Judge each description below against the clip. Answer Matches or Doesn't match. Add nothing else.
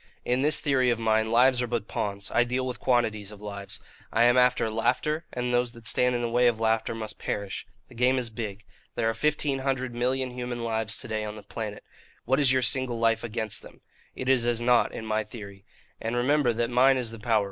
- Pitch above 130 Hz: Doesn't match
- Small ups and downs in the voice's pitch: Matches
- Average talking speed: Doesn't match